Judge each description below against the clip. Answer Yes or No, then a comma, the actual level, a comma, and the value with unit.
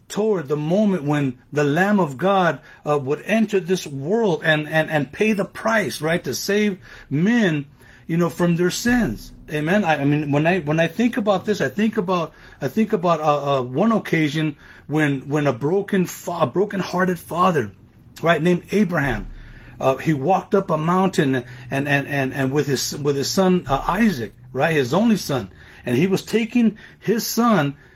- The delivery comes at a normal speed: Yes, average, 185 wpm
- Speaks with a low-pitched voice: No, medium, 165 Hz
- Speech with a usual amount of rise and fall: No, wide, 5.7 semitones